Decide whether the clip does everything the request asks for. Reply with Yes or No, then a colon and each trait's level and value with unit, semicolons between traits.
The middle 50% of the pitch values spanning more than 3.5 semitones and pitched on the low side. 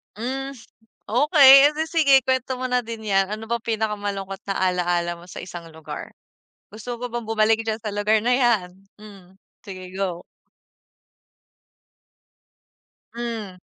No: average, 4.2 semitones; high, 220 Hz